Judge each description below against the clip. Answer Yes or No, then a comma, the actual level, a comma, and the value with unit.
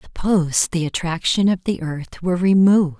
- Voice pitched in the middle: Yes, medium, 175 Hz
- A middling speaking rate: Yes, average, 160 wpm